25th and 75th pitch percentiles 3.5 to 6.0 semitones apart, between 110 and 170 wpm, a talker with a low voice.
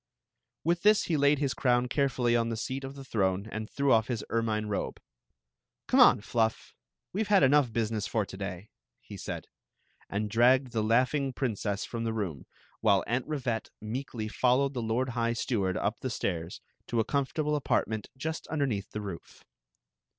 No: average, 4.0 semitones; average, 185 wpm; low, 115 Hz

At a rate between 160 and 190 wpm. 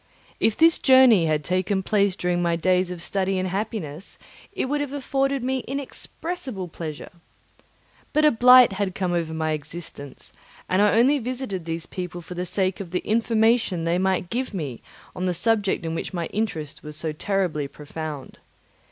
Yes: average, 175 wpm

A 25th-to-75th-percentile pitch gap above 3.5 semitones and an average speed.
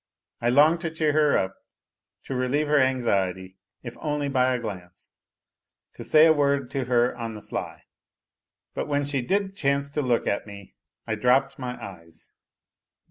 Yes: average, 4.1 semitones; average, 170 wpm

